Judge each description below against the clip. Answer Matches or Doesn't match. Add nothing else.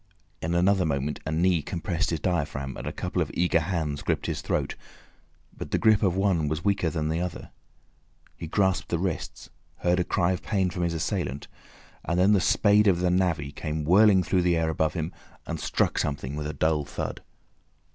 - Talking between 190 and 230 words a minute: Matches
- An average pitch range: Matches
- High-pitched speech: Doesn't match